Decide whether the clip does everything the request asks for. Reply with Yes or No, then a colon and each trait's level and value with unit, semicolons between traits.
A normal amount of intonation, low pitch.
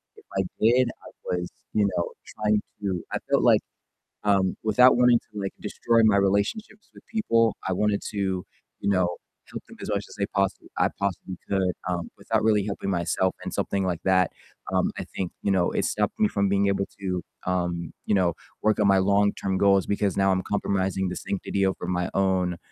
No: narrow, 1.9 semitones; low, 100 Hz